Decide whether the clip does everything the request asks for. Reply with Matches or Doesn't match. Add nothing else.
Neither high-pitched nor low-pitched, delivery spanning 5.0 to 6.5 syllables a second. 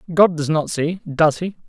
Doesn't match